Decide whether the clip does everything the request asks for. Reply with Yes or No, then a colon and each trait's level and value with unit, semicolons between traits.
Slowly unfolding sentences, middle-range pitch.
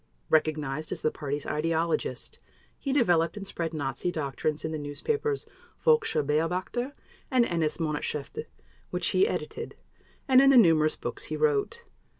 No: average, 145 wpm; medium, 165 Hz